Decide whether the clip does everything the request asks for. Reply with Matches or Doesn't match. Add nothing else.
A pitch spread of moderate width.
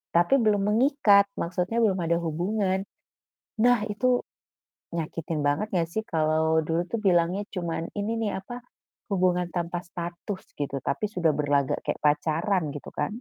Matches